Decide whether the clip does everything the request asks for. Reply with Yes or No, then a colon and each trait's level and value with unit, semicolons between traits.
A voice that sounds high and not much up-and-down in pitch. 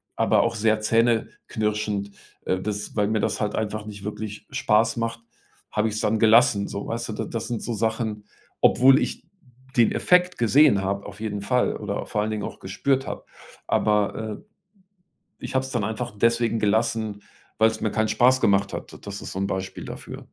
No: low, 110 Hz; narrow, 2.0 semitones